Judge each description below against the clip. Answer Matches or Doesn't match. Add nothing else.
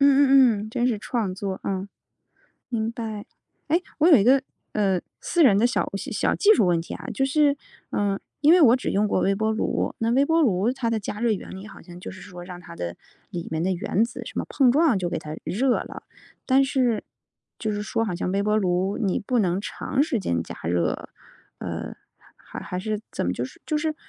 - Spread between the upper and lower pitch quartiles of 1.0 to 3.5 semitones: Doesn't match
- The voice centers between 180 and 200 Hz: Doesn't match